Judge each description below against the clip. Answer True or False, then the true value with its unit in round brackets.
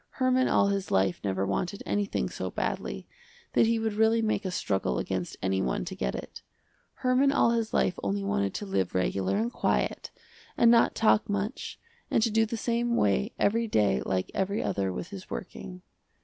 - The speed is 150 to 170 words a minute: False (190 wpm)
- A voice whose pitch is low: False (195 Hz)